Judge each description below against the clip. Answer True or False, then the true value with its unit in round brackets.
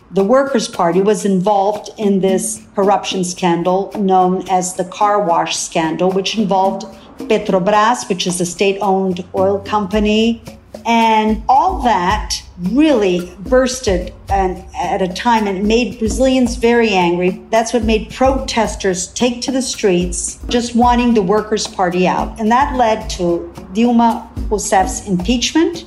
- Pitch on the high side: True (205 Hz)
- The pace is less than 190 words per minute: True (135 wpm)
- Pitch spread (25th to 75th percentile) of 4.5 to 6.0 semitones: False (3.6 semitones)